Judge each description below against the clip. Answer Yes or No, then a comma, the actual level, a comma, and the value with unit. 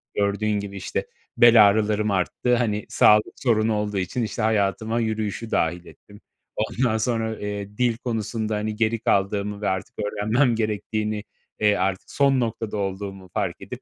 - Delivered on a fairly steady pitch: Yes, narrow, 1.8 semitones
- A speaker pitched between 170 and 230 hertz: No, low, 105 Hz